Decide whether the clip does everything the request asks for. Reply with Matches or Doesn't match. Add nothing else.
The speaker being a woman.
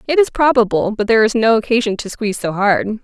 Matches